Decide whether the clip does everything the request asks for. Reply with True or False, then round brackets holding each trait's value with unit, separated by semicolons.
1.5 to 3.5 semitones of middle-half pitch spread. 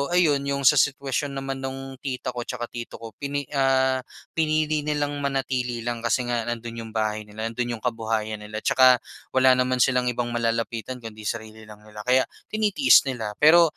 True (3.1 semitones)